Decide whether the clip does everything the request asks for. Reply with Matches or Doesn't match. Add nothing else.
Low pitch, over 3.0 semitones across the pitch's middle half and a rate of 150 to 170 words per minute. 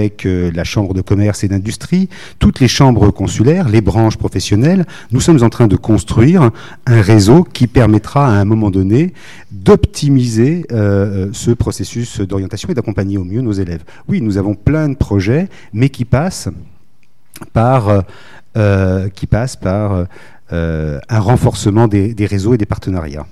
Matches